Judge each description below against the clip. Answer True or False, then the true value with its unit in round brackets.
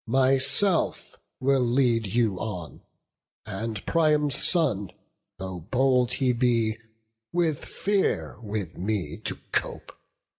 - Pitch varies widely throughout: False (4.5 semitones)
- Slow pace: True (105 wpm)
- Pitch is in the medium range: False (120 Hz)